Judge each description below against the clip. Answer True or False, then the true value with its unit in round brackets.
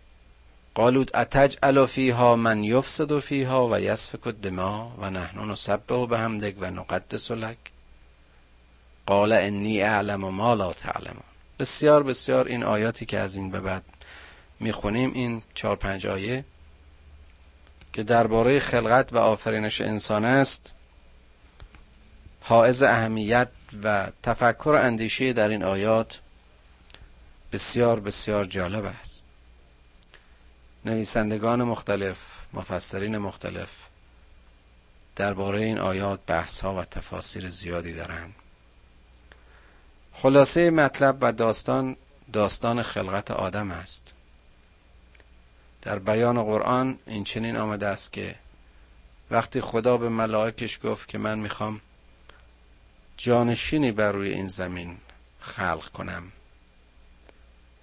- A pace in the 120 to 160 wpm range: False (110 wpm)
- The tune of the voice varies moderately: False (8.0 semitones)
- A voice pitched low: True (100 Hz)